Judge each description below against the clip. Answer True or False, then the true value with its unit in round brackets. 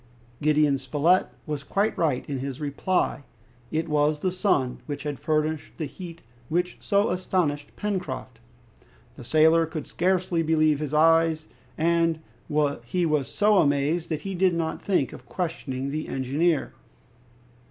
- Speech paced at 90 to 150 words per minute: True (140 wpm)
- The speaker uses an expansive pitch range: False (3.3 semitones)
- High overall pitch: False (155 Hz)